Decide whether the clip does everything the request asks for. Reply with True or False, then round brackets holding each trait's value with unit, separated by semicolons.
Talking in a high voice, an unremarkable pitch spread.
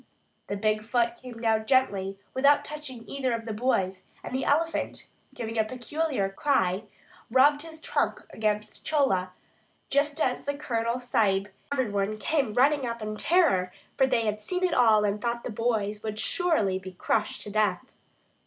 True (230 Hz; 4.5 semitones)